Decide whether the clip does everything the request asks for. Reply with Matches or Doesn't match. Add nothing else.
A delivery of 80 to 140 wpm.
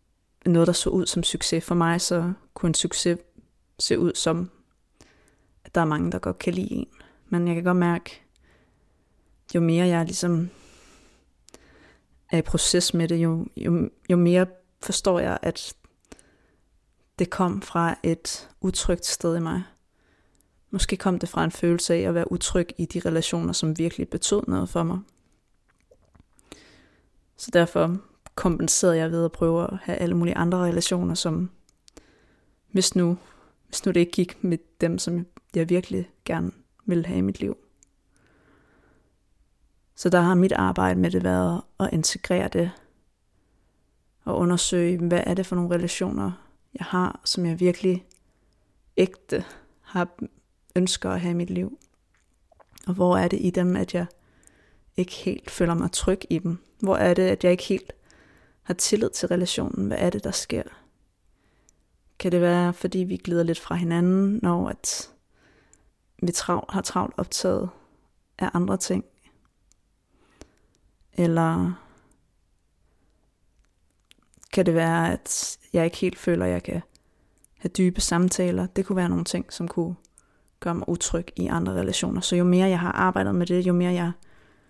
Doesn't match